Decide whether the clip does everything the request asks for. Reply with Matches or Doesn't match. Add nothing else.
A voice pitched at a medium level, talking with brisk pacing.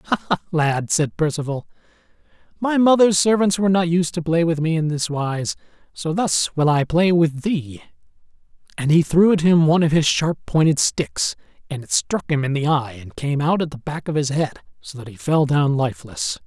Matches